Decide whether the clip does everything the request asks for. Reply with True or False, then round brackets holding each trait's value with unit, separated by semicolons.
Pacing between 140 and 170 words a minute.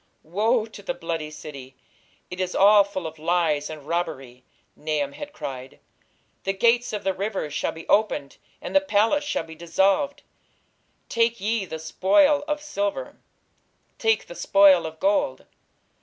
True (155 wpm)